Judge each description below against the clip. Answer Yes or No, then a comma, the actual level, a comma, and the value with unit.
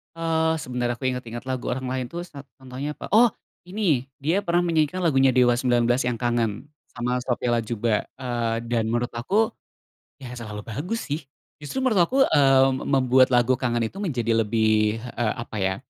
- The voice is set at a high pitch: No, low, 125 Hz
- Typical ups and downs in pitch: Yes, average, 4.0 semitones